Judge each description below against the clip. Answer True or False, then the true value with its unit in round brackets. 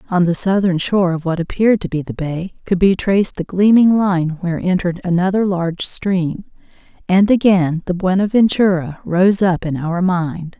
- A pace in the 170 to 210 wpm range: True (175 wpm)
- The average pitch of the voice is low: False (180 Hz)